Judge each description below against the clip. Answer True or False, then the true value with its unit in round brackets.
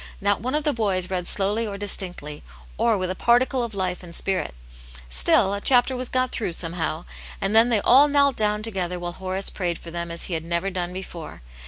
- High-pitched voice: True (195 Hz)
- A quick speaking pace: True (215 wpm)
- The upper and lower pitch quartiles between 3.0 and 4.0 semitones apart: False (4.5 semitones)